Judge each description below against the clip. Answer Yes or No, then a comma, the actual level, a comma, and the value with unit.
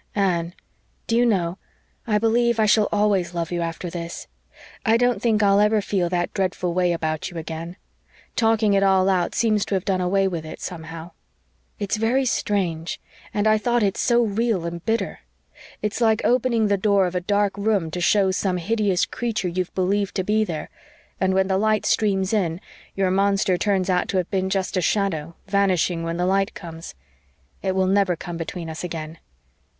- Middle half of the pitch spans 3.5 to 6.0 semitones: No, average, 3.1 semitones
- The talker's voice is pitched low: No, high, 190 Hz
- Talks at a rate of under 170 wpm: No, average, 190 wpm